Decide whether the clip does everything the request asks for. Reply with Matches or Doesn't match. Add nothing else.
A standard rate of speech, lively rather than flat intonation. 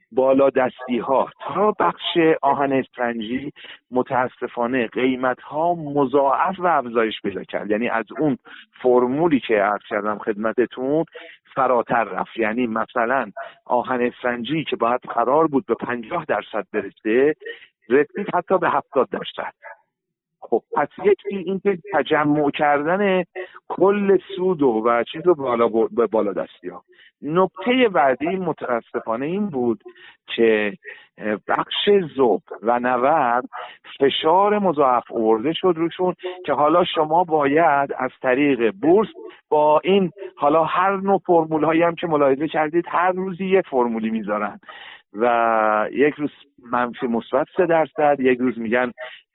Matches